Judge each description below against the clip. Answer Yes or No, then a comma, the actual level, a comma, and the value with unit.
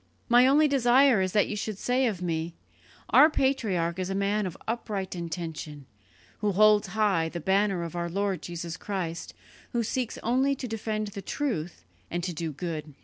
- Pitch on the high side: Yes, high, 195 Hz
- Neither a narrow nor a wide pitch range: Yes, average, 4.9 semitones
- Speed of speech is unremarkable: Yes, average, 180 wpm